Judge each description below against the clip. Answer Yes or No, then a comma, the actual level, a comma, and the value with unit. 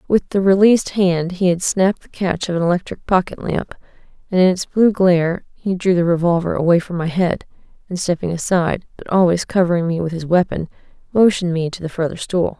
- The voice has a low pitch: No, medium, 180 Hz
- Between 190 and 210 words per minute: Yes, fast, 205 wpm